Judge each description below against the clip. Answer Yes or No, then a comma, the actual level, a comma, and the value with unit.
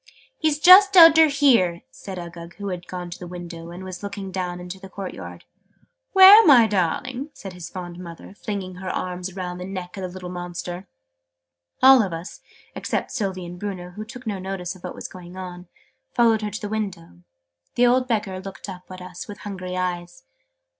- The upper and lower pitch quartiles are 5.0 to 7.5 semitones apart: No, average, 3.0 semitones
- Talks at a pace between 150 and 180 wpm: No, average, 195 wpm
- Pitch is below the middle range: No, medium, 185 Hz